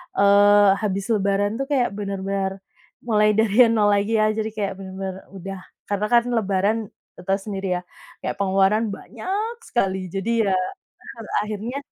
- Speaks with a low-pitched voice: No, high, 205 Hz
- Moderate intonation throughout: No, narrow, 2.2 semitones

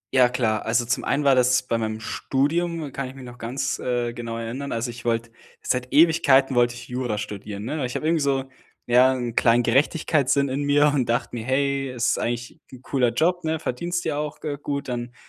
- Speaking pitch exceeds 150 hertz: No, low, 125 Hz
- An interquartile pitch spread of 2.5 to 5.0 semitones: Yes, average, 2.8 semitones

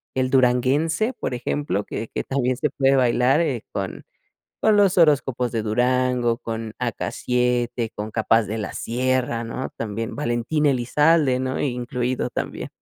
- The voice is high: No, low, 125 Hz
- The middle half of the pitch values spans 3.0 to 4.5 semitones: No, narrow, 2.5 semitones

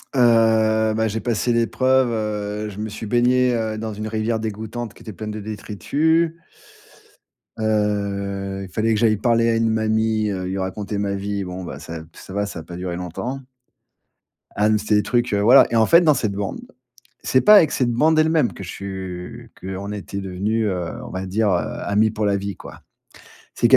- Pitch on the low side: Yes, low, 110 Hz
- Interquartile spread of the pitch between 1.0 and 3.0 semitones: Yes, narrow, 2.5 semitones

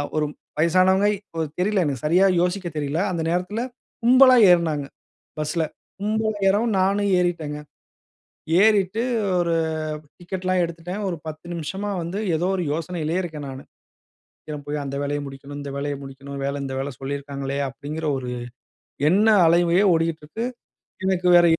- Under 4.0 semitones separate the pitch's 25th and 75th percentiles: No, average, 4.5 semitones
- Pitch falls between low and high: Yes, medium, 170 Hz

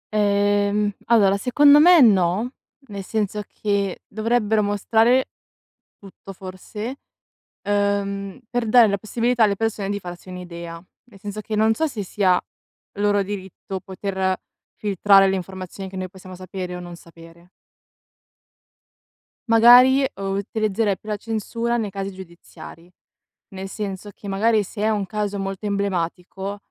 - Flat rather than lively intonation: Yes, narrow, 2.3 semitones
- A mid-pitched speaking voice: No, high, 200 Hz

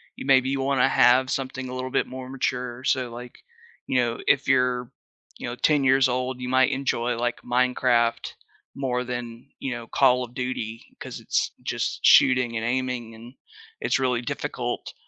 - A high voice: No, low, 125 Hz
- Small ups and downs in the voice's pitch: Yes, narrow, 1.3 semitones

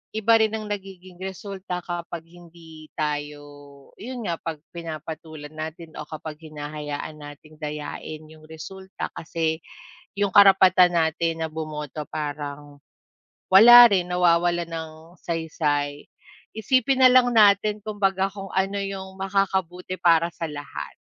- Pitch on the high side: No, medium, 170 Hz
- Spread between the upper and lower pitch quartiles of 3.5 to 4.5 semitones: Yes, average, 3.9 semitones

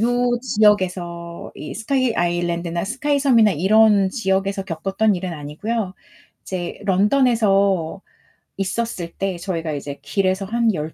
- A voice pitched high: Yes, high, 195 Hz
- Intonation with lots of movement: No, average, 4.3 semitones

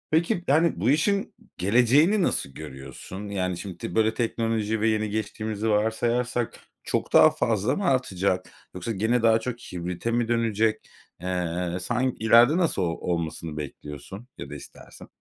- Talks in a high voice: No, low, 110 Hz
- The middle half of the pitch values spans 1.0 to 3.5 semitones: No, average, 4.7 semitones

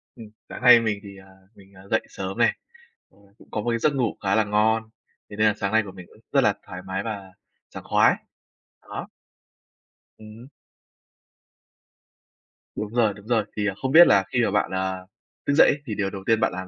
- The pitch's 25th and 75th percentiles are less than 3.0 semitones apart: Yes, narrow, 2.6 semitones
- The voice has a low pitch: Yes, low, 105 Hz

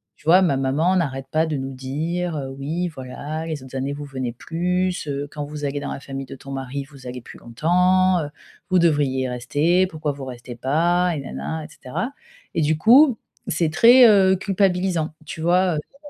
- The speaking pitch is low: No, medium, 155 Hz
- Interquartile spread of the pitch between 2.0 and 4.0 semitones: No, average, 4.8 semitones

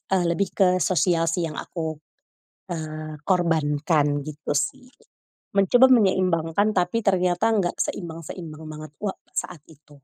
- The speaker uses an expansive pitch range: No, average, 3.3 semitones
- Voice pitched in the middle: Yes, medium, 170 Hz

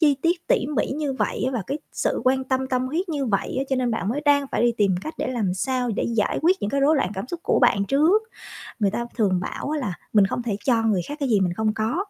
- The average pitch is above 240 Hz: Yes, very high, 255 Hz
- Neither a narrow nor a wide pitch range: Yes, average, 5.0 semitones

